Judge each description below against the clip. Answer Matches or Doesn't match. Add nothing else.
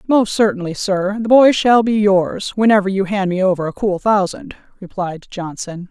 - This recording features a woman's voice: Matches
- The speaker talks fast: Doesn't match